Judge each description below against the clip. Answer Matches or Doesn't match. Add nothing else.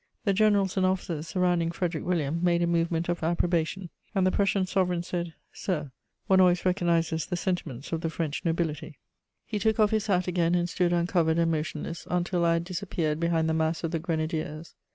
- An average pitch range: Doesn't match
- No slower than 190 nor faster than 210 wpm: Matches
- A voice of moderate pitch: Matches